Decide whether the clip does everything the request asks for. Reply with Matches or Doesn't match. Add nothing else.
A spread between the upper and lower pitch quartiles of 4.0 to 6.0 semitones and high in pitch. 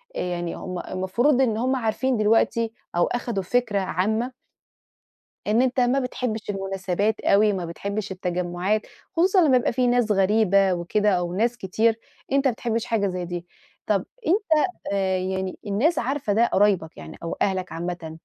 Matches